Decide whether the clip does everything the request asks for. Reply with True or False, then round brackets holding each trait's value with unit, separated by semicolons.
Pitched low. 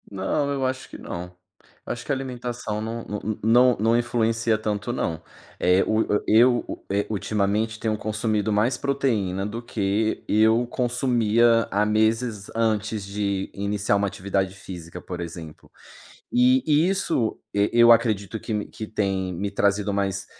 True (110 Hz)